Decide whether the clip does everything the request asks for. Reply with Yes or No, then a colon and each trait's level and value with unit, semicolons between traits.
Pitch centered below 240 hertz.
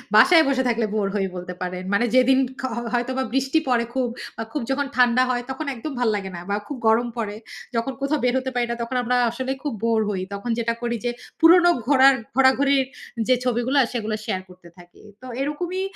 No: very high, 250 Hz